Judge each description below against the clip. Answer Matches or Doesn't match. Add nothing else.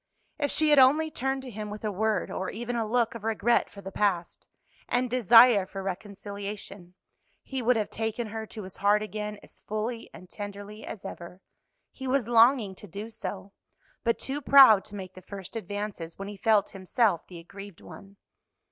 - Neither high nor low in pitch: Doesn't match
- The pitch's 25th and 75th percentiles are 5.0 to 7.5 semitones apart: Doesn't match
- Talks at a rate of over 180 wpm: Matches